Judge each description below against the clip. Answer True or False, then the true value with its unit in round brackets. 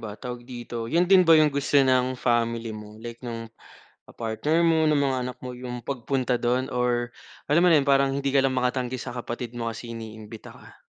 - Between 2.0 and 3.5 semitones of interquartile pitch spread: True (2.8 semitones)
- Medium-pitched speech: False (125 Hz)